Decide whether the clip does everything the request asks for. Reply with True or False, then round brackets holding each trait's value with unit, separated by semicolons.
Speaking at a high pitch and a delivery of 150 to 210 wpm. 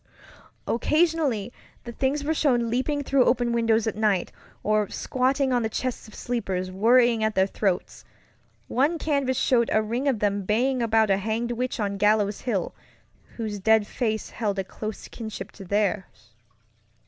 True (225 Hz; 160 wpm)